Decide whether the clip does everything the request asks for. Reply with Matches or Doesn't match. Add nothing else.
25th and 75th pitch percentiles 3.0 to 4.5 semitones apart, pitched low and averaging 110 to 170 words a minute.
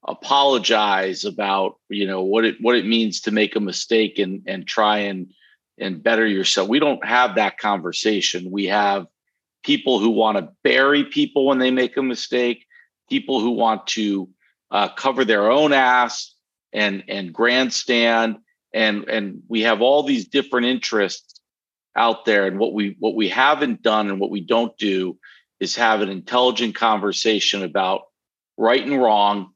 Matches